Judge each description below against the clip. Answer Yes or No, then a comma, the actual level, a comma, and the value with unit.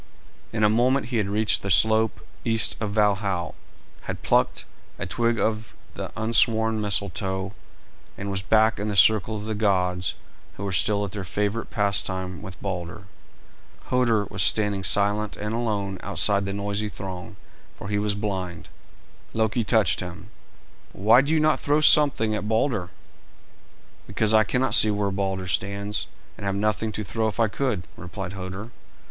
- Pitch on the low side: Yes, low, 105 Hz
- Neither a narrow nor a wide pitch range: No, narrow, 2.2 semitones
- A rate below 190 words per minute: Yes, average, 165 wpm